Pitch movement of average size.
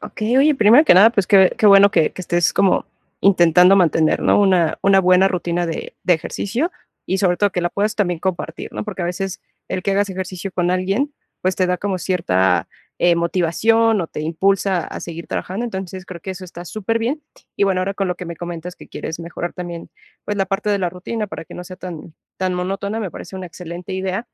No: narrow, 2.3 semitones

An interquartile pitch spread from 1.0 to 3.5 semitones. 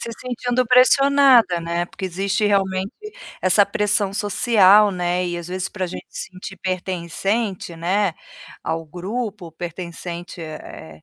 Yes: average, 3.2 semitones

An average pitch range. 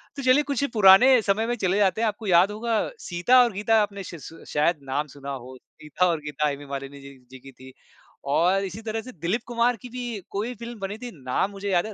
No: wide, 7.1 semitones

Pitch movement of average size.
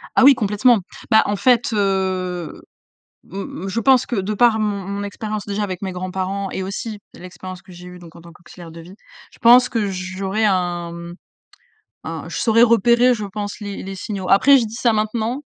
Yes: average, 3.3 semitones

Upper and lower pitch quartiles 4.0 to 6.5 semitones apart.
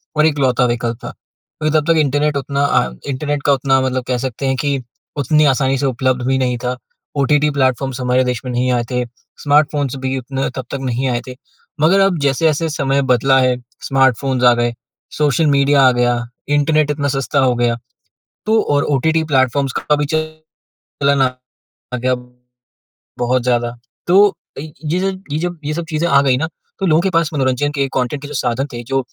No: average, 2.8 semitones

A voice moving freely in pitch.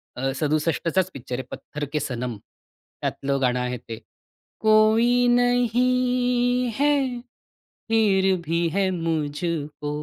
Yes: wide, 8.8 semitones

